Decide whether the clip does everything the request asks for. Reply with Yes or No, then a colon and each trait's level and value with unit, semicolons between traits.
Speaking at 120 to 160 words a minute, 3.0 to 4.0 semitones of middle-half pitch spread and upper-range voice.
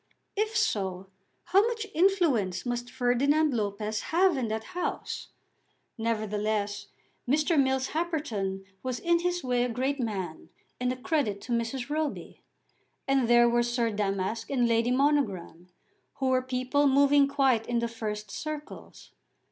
No: average, 140 wpm; average, 4.9 semitones; very high, 250 Hz